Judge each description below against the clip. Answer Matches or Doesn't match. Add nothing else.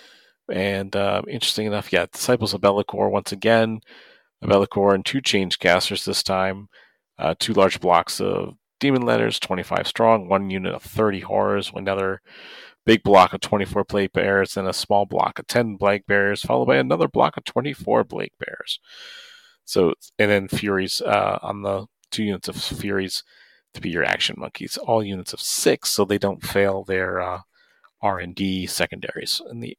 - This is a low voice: Matches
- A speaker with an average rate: Matches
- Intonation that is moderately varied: Doesn't match